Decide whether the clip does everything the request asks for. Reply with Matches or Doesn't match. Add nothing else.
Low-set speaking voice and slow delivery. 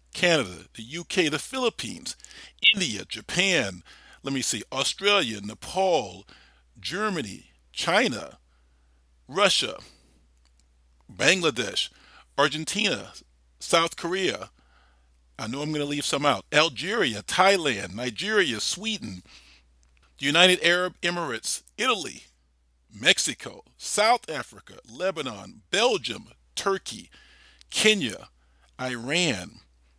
Matches